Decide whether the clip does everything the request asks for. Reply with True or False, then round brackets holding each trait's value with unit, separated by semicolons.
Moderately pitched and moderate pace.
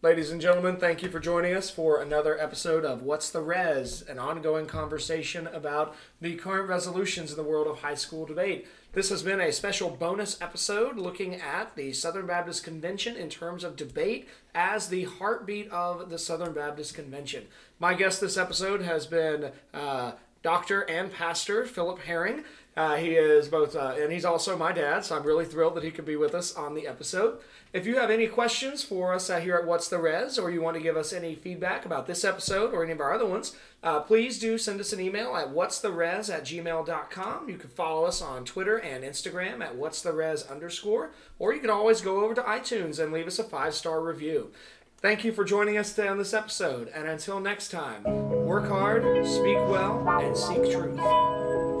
False (175 Hz; 210 wpm)